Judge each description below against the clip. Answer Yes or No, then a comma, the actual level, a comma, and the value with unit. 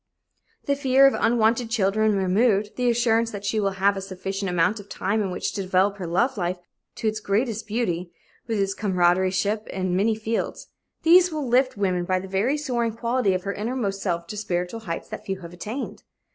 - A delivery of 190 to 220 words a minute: Yes, average, 200 wpm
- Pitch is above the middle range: Yes, high, 205 Hz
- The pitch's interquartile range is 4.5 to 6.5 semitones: No, average, 3.5 semitones